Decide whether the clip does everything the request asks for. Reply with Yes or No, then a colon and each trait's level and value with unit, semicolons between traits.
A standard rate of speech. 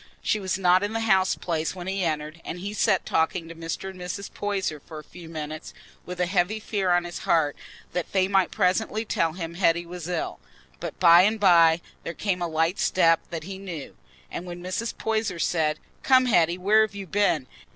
No: fast, 210 wpm